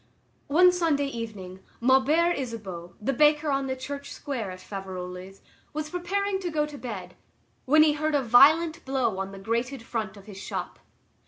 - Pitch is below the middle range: No, very high, 265 Hz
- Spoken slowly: No, average, 170 wpm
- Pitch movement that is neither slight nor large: No, wide, 7.2 semitones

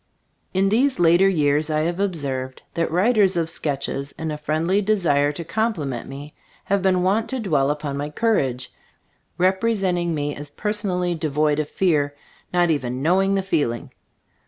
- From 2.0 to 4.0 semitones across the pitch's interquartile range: No, average, 4.9 semitones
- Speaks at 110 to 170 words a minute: Yes, average, 160 wpm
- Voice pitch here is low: No, medium, 165 Hz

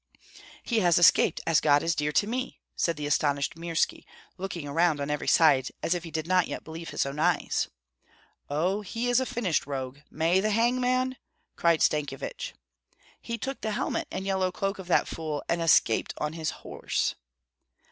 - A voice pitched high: No, medium, 170 Hz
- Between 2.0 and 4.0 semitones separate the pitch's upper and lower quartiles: No, average, 4.6 semitones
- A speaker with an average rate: Yes, average, 185 wpm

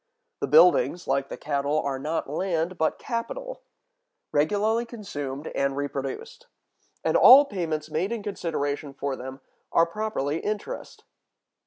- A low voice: No, medium, 160 Hz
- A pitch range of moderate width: No, wide, 7.1 semitones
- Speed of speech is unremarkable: No, slow, 130 wpm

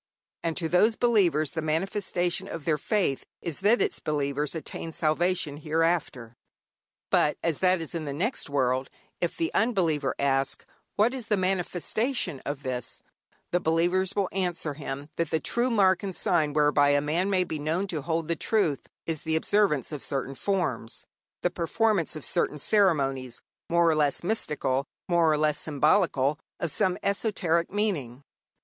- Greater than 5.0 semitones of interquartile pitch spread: No, average, 4.3 semitones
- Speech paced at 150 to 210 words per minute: Yes, average, 165 wpm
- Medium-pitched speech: Yes, medium, 165 Hz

